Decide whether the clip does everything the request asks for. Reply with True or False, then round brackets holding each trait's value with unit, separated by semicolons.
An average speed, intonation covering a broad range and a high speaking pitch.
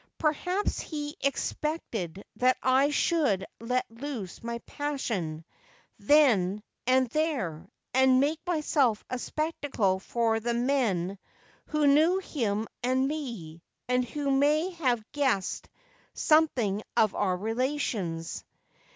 False (115 wpm; 6.0 semitones; 255 Hz)